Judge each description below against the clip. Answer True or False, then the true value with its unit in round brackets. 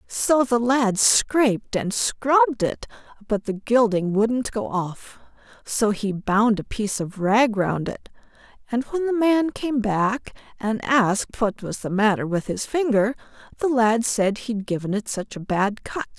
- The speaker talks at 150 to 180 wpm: True (175 wpm)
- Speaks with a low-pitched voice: False (225 Hz)